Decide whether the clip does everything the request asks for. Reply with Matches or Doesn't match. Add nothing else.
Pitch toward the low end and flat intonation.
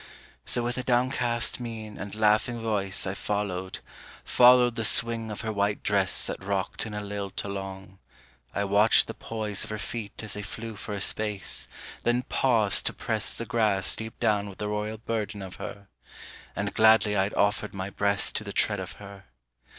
Matches